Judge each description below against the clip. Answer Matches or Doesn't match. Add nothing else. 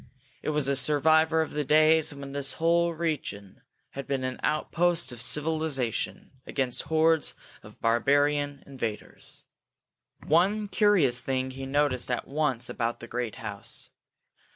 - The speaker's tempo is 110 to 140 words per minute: Matches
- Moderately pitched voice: Matches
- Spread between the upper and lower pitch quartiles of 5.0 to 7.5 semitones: Doesn't match